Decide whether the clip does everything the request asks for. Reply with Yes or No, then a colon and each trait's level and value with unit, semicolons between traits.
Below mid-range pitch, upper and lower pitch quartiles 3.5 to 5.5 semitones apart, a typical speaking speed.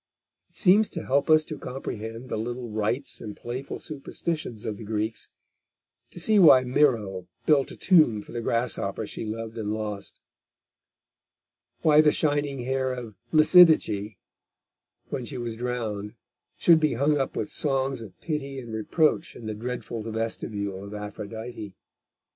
Yes: low, 120 Hz; average, 5.0 semitones; average, 150 wpm